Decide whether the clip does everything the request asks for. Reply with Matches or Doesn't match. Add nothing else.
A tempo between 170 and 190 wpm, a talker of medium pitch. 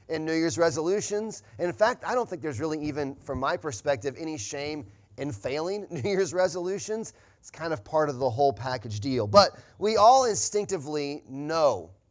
Matches